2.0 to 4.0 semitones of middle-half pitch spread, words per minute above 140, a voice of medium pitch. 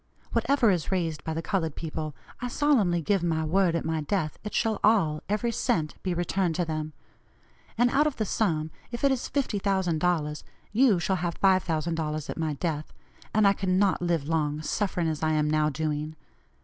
No: average, 4.4 semitones; average, 185 wpm; medium, 170 Hz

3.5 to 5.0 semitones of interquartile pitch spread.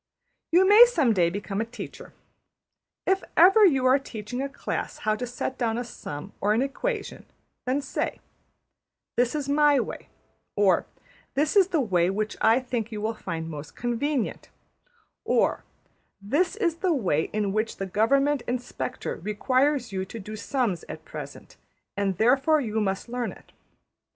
No: wide, 5.4 semitones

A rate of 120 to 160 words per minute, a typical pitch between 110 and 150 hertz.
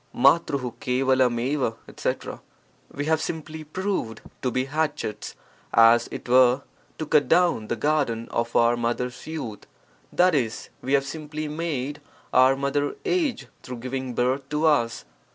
Yes: average, 140 wpm; low, 135 Hz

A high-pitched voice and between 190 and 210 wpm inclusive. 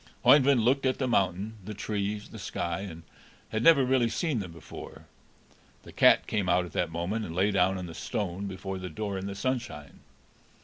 No: low, 100 Hz; average, 200 wpm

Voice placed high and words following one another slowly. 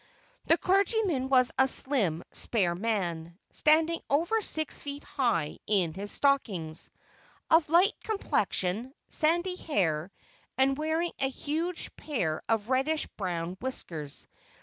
Yes: very high, 265 Hz; slow, 120 wpm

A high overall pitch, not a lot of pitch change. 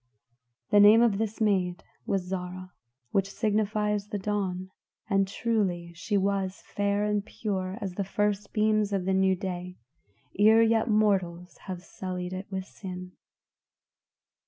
Yes: high, 195 Hz; narrow, 2.1 semitones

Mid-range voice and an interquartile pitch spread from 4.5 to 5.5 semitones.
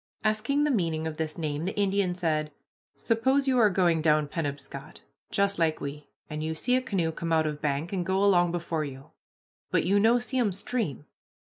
Yes: medium, 170 Hz; average, 4.8 semitones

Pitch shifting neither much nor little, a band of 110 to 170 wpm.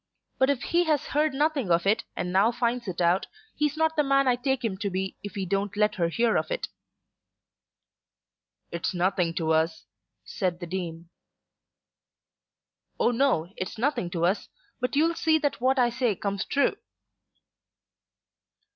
No: wide, 7.2 semitones; average, 165 wpm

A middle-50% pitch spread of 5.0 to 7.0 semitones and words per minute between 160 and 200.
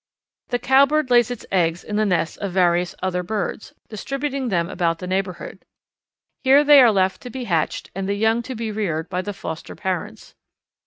Yes: average, 5.3 semitones; average, 190 wpm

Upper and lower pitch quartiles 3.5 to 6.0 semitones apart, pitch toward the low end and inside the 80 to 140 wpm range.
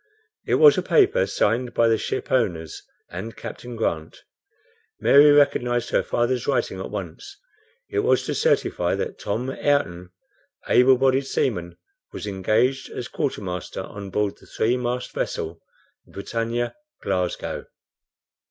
Yes: average, 5.2 semitones; low, 120 Hz; slow, 135 wpm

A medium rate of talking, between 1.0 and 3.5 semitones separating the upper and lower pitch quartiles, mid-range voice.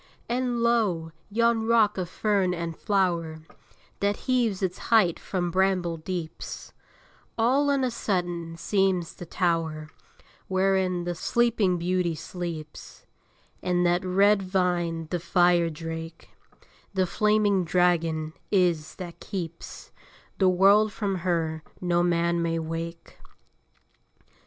No: slow, 120 wpm; average, 3.0 semitones; medium, 180 Hz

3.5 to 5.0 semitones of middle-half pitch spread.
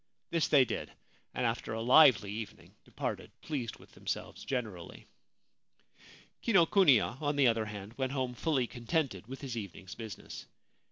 Yes: average, 4.3 semitones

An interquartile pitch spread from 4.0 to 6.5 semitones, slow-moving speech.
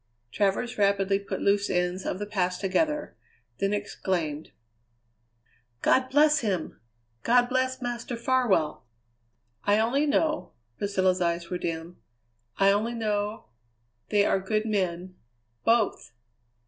Yes: average, 4.4 semitones; slow, 120 wpm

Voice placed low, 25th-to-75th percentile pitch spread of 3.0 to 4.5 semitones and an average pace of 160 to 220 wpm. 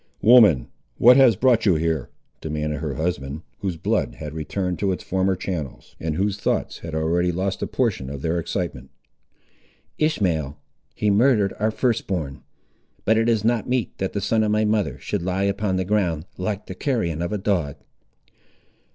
No: very low, 95 Hz; average, 5.0 semitones; average, 175 wpm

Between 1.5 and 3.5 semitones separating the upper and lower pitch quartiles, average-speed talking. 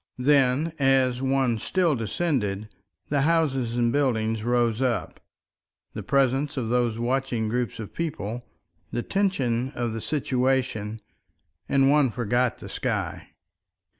No: average, 2.8 semitones; slow, 125 wpm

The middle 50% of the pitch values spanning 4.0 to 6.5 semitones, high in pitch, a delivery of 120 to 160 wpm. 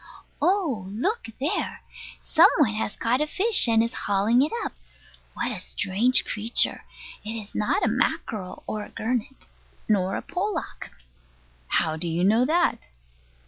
Yes: average, 5.2 semitones; high, 225 Hz; average, 150 wpm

